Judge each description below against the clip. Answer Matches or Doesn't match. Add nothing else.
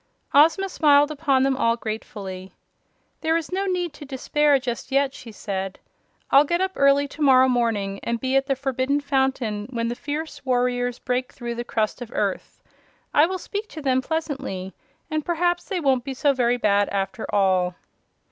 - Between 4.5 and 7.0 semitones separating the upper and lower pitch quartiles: Doesn't match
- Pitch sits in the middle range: Doesn't match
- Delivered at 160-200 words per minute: Matches